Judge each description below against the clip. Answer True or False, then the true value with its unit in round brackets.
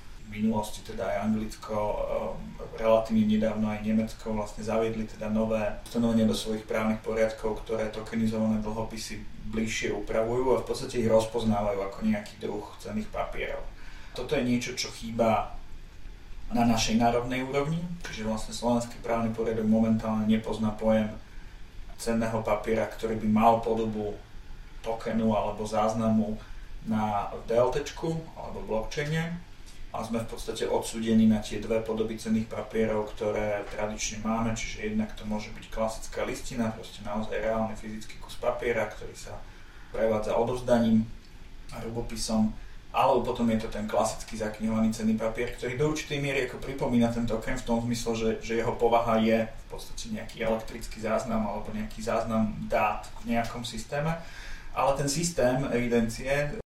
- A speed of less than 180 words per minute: True (145 wpm)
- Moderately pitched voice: False (110 Hz)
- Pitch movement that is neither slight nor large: False (1.3 semitones)